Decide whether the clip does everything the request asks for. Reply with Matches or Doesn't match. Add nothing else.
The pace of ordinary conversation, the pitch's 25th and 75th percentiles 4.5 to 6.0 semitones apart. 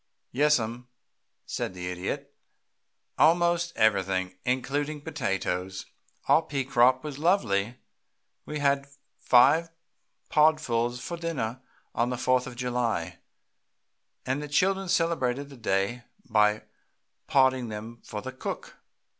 Doesn't match